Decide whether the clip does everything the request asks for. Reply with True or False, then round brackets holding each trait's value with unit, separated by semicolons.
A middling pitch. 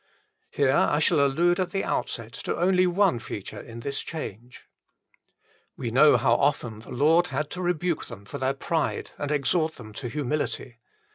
True (145 Hz)